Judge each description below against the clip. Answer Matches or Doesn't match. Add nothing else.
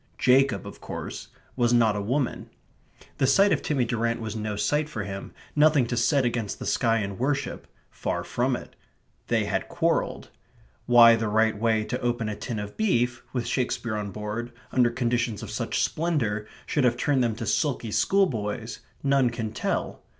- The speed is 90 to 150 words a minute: Doesn't match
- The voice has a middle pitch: Doesn't match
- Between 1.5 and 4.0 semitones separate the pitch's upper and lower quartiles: Matches